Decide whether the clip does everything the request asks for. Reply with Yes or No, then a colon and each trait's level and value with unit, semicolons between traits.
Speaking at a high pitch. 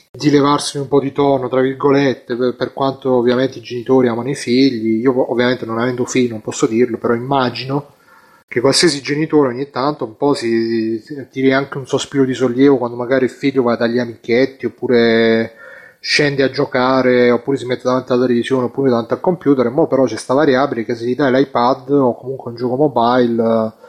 No: low, 130 Hz